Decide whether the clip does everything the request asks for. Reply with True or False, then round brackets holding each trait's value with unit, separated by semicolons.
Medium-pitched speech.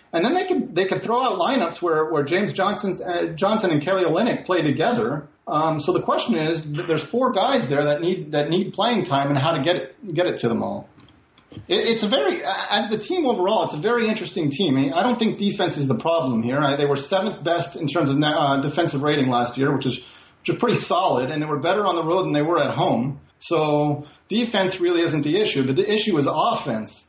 True (170 Hz)